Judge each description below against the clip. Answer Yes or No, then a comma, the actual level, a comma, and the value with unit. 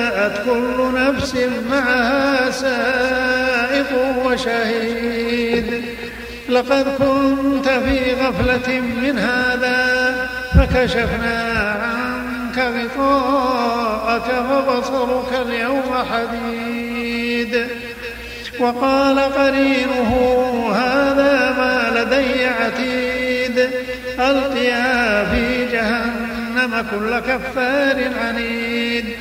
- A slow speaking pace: Yes, slow, 60 wpm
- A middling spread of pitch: No, narrow, 1.5 semitones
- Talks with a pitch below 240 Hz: No, very high, 250 Hz